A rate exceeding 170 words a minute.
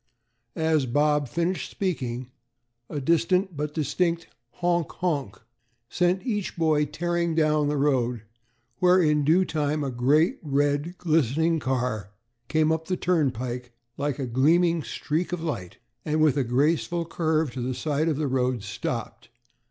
No: average, 145 wpm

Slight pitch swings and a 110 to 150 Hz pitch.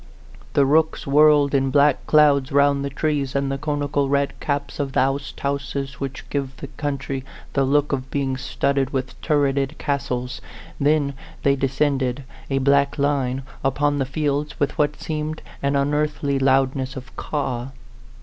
Yes: narrow, 1.2 semitones; medium, 140 Hz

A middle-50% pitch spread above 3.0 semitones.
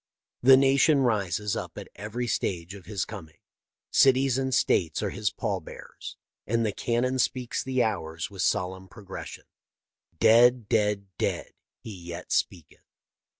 Yes: average, 4.9 semitones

